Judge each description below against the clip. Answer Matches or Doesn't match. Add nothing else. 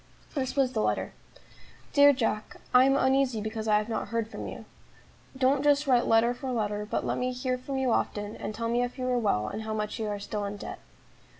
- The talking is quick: Matches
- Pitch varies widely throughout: Doesn't match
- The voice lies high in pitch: Matches